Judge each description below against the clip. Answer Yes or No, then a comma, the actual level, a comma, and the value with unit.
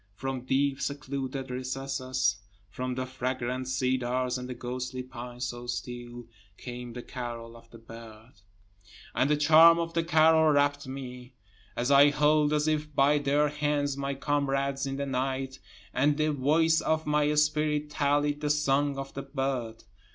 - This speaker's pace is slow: No, average, 160 wpm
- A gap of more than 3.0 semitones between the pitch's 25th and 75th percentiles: No, narrow, 2.6 semitones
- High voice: No, low, 135 Hz